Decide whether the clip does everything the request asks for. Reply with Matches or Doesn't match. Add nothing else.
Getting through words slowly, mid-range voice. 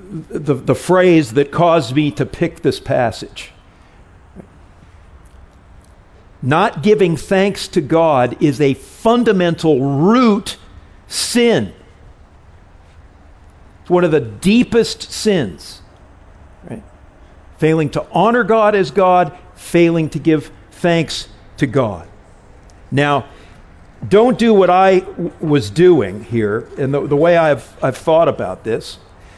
Matches